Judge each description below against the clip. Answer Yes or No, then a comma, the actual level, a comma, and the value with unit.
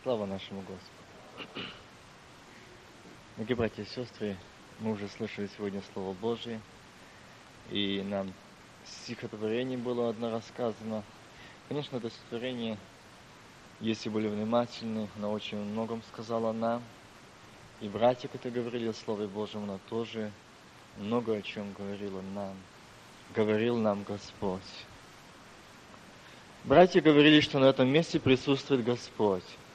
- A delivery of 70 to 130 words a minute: Yes, slow, 110 wpm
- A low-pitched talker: Yes, low, 110 Hz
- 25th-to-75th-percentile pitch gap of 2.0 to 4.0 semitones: Yes, average, 2.7 semitones